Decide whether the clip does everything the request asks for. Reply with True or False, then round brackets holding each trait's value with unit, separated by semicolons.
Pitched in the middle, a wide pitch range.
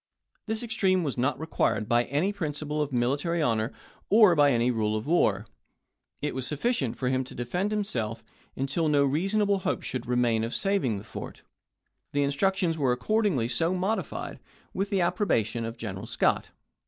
True (145 Hz; 7.6 semitones)